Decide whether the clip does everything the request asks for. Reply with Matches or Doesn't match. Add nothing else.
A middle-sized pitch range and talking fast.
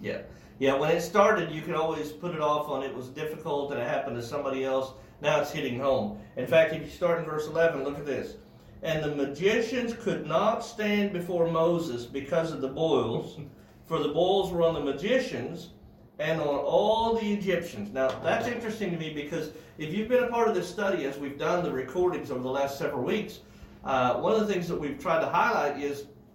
Matches